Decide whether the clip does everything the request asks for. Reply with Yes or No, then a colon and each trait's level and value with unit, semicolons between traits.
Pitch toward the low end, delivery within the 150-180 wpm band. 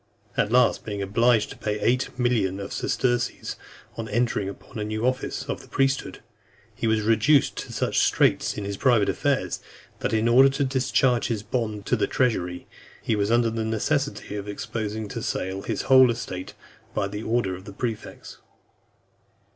Yes: low, 110 Hz; average, 170 wpm